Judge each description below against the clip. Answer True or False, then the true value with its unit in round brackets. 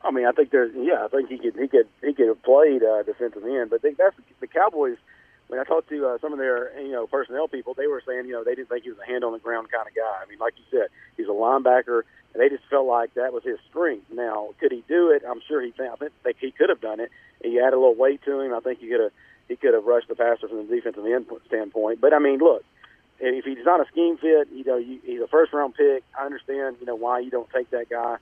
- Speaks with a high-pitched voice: False (140 Hz)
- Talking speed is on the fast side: True (285 wpm)